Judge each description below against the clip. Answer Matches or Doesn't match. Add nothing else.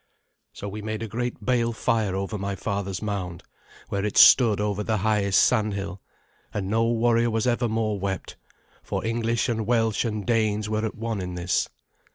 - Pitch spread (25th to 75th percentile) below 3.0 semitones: Matches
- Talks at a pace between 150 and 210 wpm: Matches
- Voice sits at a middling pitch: Doesn't match